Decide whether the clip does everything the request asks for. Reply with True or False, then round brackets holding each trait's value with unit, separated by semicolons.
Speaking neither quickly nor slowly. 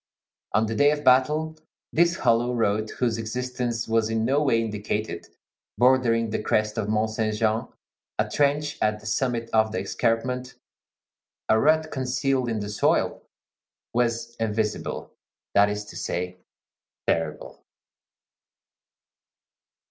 False (130 wpm)